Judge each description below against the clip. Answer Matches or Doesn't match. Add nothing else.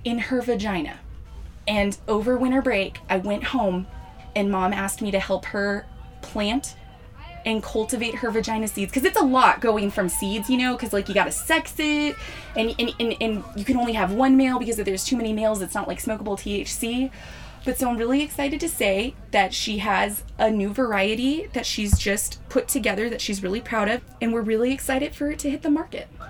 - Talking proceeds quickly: Matches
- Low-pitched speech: Doesn't match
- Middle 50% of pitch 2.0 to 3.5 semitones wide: Doesn't match